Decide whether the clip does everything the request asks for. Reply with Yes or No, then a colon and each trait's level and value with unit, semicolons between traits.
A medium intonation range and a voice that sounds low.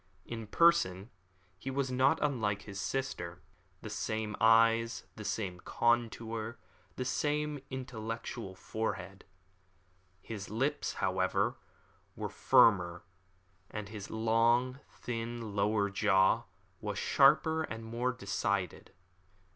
Yes: average, 3.8 semitones; low, 115 Hz